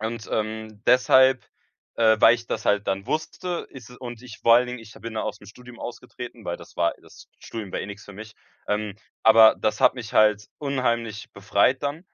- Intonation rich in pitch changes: No, average, 2.7 semitones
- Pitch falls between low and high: No, low, 115 Hz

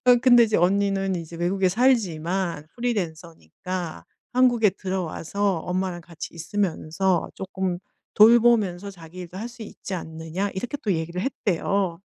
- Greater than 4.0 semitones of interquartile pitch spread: No, average, 3.3 semitones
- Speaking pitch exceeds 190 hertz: No, medium, 185 Hz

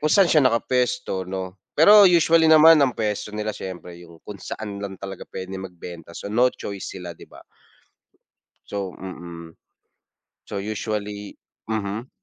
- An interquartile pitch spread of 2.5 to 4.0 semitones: No, average, 4.8 semitones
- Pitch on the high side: No, low, 100 Hz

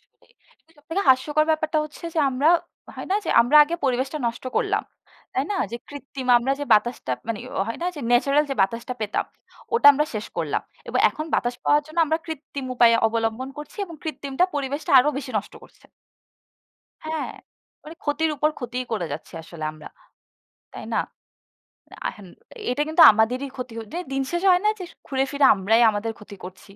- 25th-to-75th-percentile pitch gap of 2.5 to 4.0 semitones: No, average, 4.8 semitones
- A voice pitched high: Yes, very high, 270 Hz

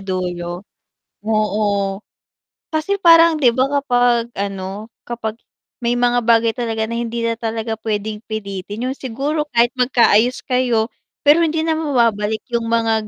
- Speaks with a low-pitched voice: No, high, 230 Hz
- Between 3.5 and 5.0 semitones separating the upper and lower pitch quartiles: No, average, 2.9 semitones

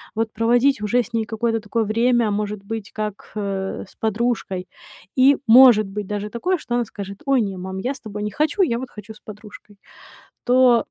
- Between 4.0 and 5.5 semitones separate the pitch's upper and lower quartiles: No, average, 2.7 semitones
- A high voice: Yes, high, 220 Hz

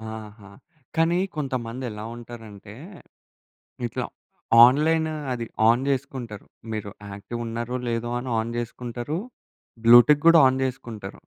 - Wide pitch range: No, average, 2.9 semitones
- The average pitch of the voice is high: No, low, 120 Hz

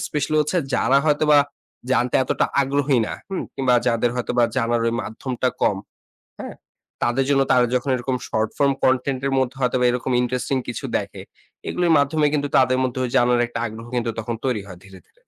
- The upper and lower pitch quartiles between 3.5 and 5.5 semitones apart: No, narrow, 2.6 semitones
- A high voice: No, low, 125 Hz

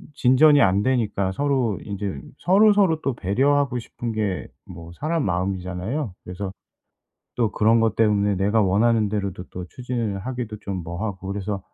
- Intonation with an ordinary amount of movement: Yes, average, 4.6 semitones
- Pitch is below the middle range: Yes, low, 105 Hz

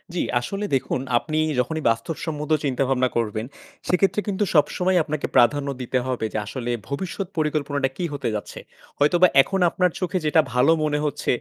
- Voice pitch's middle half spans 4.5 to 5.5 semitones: Yes, average, 5.2 semitones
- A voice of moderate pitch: Yes, medium, 150 Hz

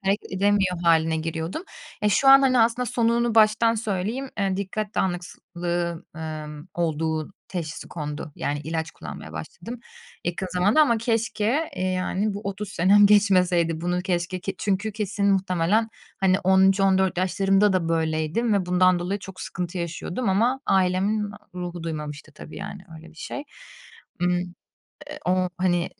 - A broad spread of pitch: No, average, 3.4 semitones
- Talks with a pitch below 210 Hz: Yes, medium, 185 Hz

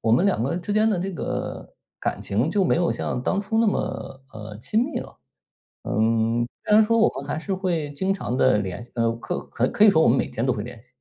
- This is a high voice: No, medium, 155 Hz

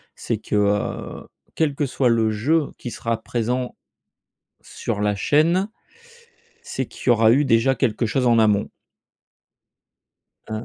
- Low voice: Yes, low, 120 Hz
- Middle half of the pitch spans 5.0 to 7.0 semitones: No, average, 3.7 semitones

